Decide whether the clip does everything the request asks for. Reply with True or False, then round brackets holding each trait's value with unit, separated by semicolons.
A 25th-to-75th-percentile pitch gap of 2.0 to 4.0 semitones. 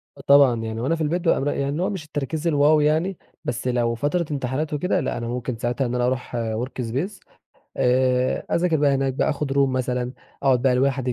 True (3.3 semitones)